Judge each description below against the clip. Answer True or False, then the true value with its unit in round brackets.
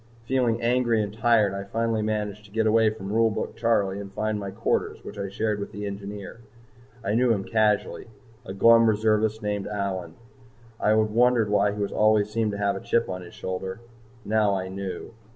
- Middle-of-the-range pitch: False (105 Hz)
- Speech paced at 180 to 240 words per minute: True (195 wpm)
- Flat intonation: True (2.1 semitones)